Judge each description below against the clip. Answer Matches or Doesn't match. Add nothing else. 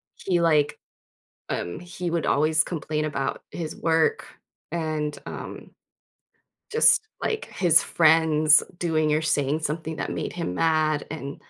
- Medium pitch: Matches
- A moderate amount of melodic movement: Doesn't match